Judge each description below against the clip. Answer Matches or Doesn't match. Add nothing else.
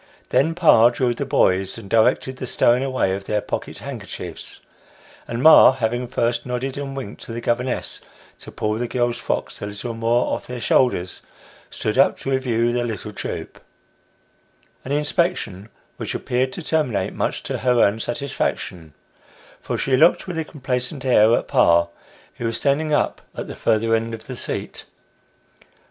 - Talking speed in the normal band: Matches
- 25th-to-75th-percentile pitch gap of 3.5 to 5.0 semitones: Doesn't match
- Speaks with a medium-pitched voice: Doesn't match